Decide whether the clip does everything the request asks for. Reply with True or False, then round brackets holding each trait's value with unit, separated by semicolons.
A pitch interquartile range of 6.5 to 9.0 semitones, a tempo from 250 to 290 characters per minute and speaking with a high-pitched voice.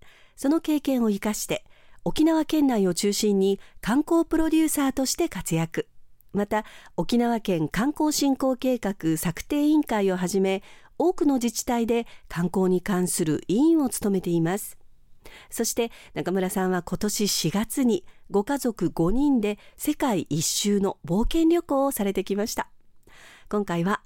True (6.9 semitones; 275 characters per minute; 210 Hz)